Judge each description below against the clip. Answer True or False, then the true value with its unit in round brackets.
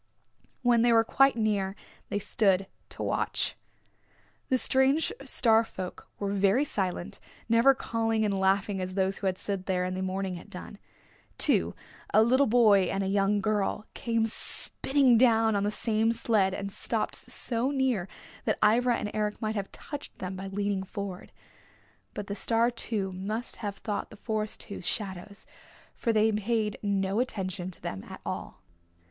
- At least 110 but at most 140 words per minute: False (165 wpm)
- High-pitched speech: True (210 Hz)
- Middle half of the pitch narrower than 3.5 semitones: True (3.0 semitones)